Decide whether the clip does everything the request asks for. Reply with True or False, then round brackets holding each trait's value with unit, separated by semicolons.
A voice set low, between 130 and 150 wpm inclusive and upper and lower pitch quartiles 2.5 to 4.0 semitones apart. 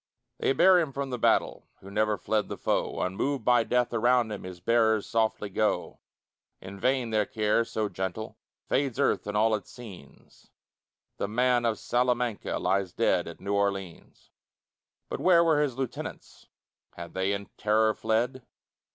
False (110 Hz; 160 wpm; 3.6 semitones)